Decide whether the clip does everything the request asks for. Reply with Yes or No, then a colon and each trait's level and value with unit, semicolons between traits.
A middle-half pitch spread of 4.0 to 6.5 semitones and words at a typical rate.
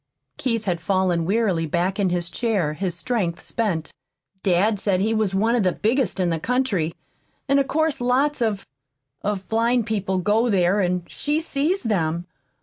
Yes: average, 4.7 semitones; average, 170 wpm